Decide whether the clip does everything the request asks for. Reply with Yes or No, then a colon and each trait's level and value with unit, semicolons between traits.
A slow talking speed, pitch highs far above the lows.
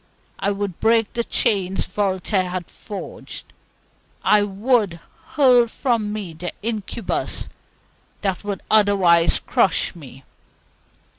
No: slow, 105 wpm; average, 3.2 semitones